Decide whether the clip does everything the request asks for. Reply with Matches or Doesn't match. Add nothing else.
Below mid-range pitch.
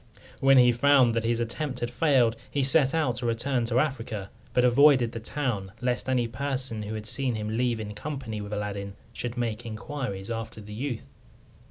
Matches